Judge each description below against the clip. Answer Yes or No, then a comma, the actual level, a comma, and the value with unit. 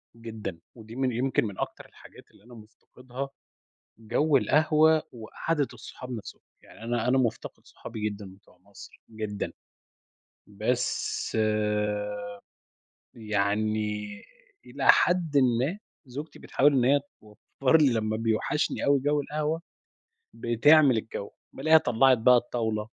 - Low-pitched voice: Yes, low, 120 Hz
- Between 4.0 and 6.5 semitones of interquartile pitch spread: Yes, average, 4.3 semitones